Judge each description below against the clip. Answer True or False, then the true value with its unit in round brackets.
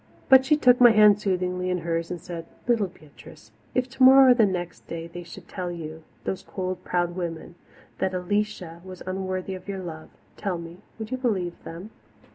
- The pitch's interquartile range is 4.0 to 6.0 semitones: False (3.5 semitones)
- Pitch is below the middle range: False (185 Hz)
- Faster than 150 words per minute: True (190 wpm)